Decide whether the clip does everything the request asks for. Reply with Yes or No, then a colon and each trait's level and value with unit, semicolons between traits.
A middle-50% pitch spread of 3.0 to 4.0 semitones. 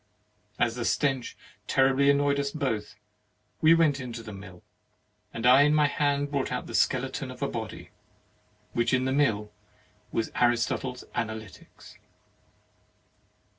Yes: average, 3.6 semitones